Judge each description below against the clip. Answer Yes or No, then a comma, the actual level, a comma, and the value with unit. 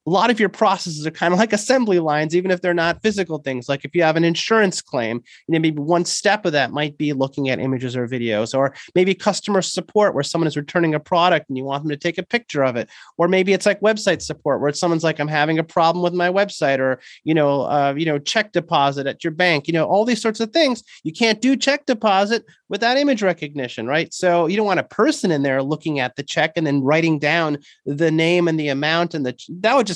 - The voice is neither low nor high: Yes, medium, 165 Hz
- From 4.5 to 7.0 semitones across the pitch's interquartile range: Yes, average, 4.8 semitones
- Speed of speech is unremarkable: No, fast, 255 wpm